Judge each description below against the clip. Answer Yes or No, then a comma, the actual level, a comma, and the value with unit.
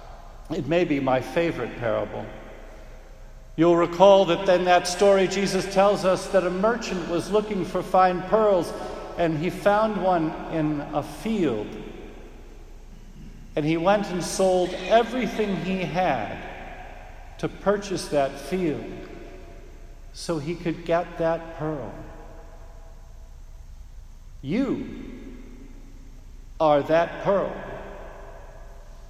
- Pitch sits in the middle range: Yes, medium, 170 Hz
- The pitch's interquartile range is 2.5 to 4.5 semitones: No, average, 4.9 semitones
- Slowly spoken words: Yes, slow, 105 wpm